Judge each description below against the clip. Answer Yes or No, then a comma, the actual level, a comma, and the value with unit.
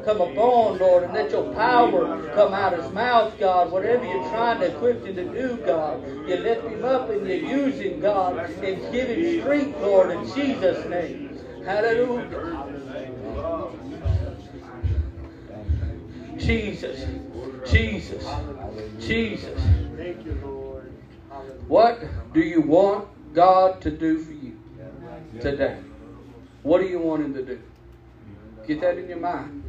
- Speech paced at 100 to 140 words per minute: Yes, slow, 135 wpm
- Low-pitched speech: No, medium, 180 Hz